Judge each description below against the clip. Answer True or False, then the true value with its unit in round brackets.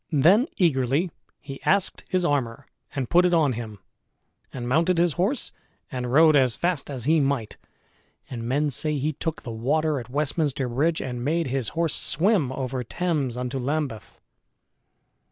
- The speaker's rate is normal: True (160 wpm)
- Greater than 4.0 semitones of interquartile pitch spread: True (4.5 semitones)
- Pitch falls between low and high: True (145 Hz)